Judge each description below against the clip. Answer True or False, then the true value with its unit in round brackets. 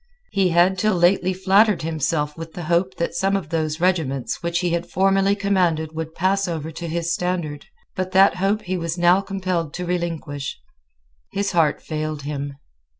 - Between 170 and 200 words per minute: True (175 wpm)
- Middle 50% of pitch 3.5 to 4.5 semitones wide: False (2.9 semitones)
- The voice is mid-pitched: True (175 Hz)